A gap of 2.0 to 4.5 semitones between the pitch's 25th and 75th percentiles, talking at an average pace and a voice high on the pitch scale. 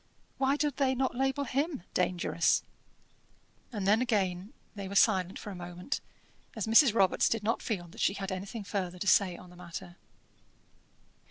No: average, 4.9 semitones; average, 170 wpm; high, 200 Hz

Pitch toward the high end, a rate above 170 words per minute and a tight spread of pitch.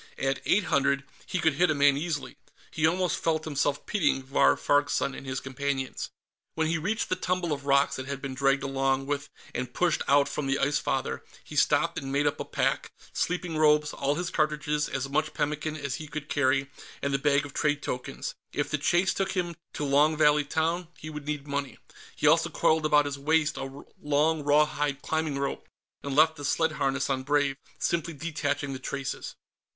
No: medium, 145 Hz; average, 200 wpm; narrow, 2.1 semitones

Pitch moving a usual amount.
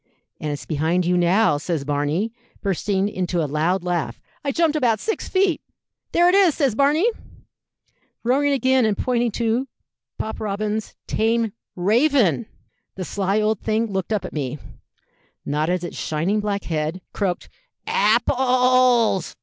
No: wide, 6.1 semitones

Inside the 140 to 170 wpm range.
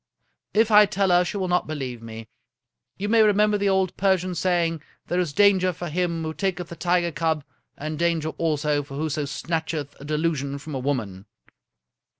No: average, 200 wpm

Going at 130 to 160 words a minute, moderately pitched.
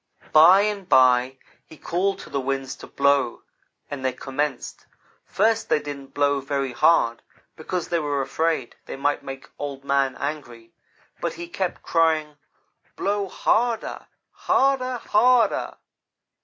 Yes: slow, 135 wpm; medium, 145 Hz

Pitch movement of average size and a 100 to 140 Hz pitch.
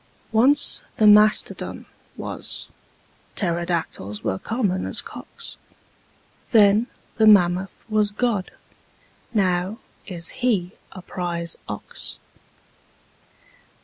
No: average, 3.6 semitones; high, 195 Hz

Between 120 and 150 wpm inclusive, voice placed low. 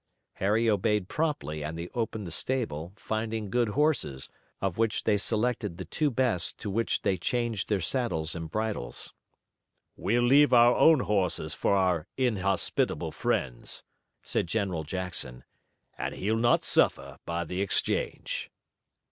Yes: average, 140 wpm; low, 105 Hz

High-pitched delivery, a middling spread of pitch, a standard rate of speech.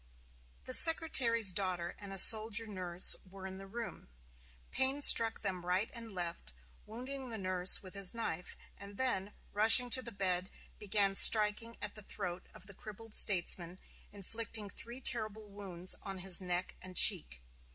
Yes: high, 200 Hz; average, 3.5 semitones; average, 160 wpm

